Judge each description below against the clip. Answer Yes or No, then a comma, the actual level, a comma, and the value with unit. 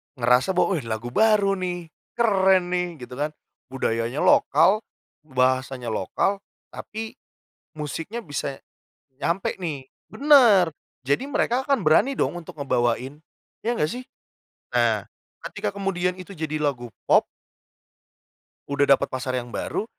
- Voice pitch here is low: No, medium, 160 Hz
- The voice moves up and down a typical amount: No, wide, 6.9 semitones